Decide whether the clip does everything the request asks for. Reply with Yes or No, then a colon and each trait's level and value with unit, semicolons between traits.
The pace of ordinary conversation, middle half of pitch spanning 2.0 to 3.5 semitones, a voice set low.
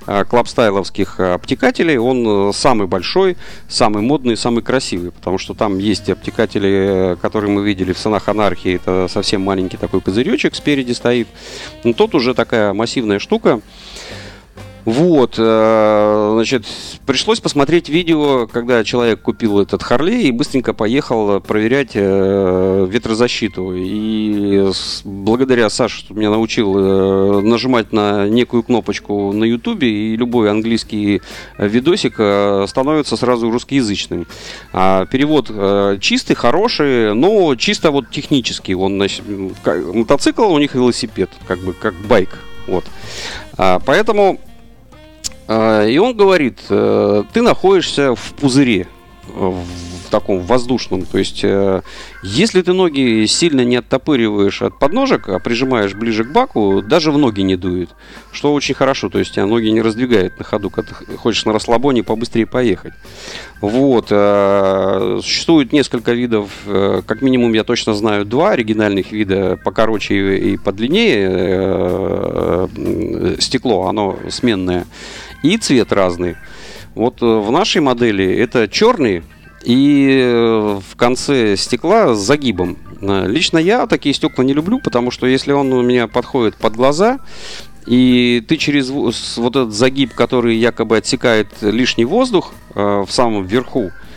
No: average, 125 wpm; average, 4.4 semitones; low, 110 Hz